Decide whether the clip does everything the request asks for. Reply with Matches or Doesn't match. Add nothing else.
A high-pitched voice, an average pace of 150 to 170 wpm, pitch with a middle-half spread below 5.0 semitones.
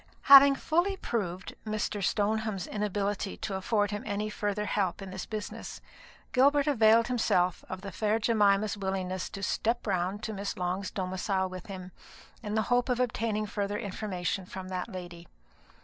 Matches